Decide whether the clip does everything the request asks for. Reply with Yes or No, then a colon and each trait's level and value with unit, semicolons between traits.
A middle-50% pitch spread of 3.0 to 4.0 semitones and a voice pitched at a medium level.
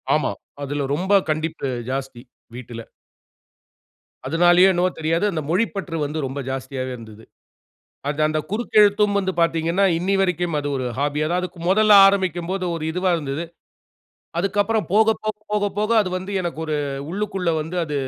No: average, 4.8 semitones; medium, 175 Hz